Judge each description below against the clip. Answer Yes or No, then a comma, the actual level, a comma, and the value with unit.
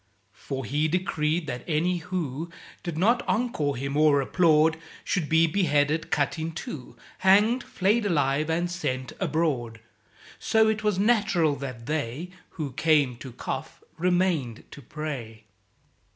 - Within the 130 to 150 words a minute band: Yes, slow, 135 wpm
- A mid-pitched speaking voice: Yes, medium, 155 Hz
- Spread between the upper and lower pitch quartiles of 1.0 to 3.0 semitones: No, average, 4.3 semitones